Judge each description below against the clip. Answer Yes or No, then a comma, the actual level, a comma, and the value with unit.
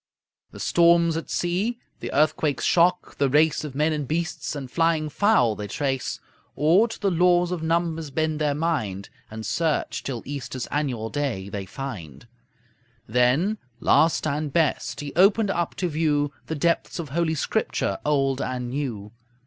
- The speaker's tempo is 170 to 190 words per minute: No, average, 160 wpm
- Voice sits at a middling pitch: Yes, medium, 150 Hz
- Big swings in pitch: No, average, 4.1 semitones